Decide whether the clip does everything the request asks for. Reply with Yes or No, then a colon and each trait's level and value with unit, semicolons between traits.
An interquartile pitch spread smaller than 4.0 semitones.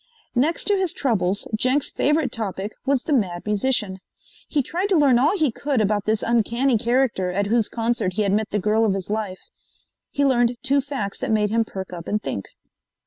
No: average, 4.8 semitones